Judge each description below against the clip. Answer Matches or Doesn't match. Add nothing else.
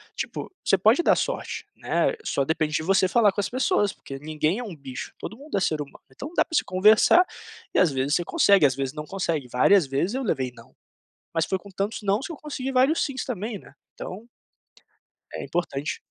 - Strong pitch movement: Matches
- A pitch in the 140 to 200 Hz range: Matches